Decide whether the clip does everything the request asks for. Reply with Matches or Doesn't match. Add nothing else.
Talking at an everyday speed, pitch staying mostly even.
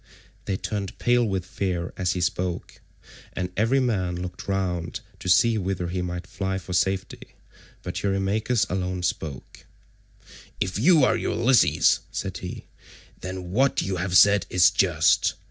Matches